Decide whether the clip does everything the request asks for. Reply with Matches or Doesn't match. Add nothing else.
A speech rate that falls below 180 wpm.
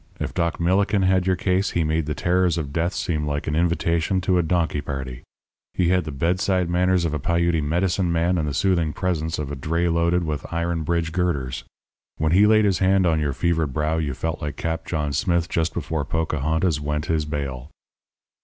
Doesn't match